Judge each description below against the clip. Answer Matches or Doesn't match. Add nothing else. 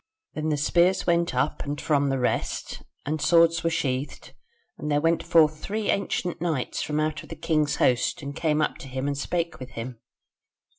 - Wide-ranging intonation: Doesn't match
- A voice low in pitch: Doesn't match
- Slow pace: Doesn't match